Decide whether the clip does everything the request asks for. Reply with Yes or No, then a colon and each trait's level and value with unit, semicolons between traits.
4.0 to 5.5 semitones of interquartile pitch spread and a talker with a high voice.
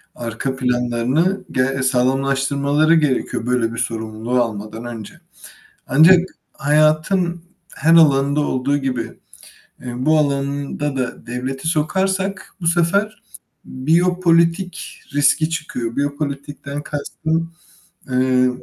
No: average, 4.3 semitones; medium, 140 Hz